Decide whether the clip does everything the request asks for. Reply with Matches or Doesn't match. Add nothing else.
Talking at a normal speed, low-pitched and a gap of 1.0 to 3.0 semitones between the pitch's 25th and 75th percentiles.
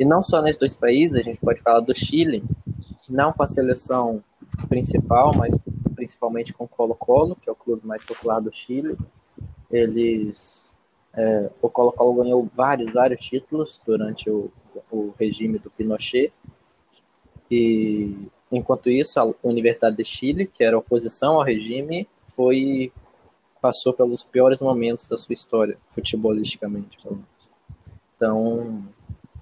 Matches